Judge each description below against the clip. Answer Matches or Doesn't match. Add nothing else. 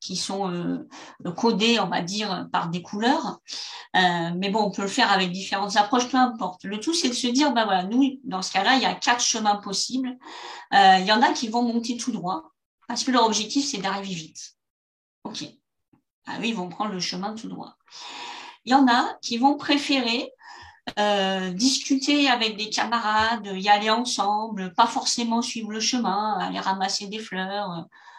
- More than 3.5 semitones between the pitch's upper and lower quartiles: Matches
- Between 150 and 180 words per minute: Doesn't match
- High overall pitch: Matches